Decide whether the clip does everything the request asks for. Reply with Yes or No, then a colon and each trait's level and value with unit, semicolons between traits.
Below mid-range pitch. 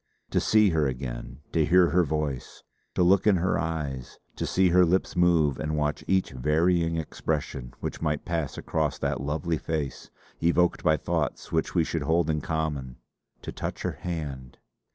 Yes: very low, 80 Hz